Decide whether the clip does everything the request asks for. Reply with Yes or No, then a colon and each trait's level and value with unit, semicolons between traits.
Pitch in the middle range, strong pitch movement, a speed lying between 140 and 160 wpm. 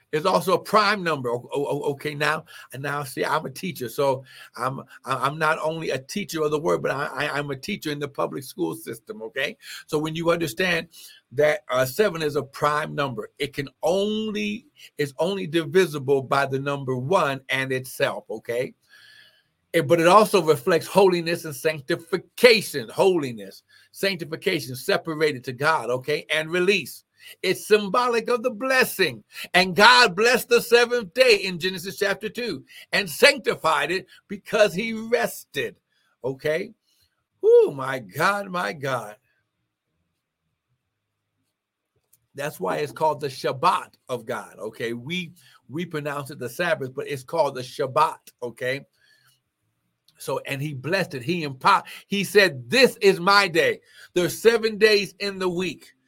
Yes: medium, 165 Hz; wide, 6.1 semitones; average, 150 wpm